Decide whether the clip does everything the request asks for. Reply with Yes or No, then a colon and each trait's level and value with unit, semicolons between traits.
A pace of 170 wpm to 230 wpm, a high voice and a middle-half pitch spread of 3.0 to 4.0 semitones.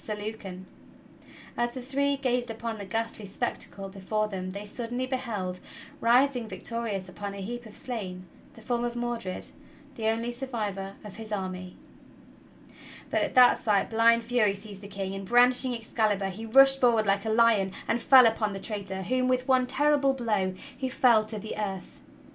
Yes: average, 175 wpm; high, 225 Hz; average, 3.6 semitones